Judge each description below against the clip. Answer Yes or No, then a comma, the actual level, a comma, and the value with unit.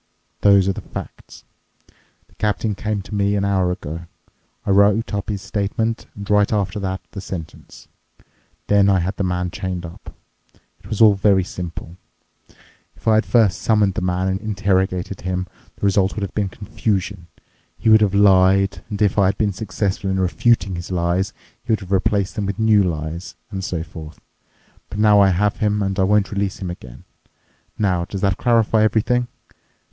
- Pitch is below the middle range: Yes, low, 100 Hz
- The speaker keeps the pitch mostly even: Yes, narrow, 2.0 semitones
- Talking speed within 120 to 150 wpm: No, average, 185 wpm